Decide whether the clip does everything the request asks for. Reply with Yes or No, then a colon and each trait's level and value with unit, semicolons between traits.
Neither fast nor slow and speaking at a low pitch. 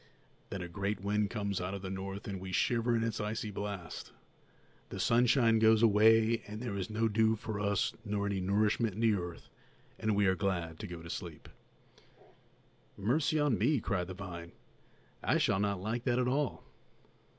Yes: average, 185 wpm; low, 105 Hz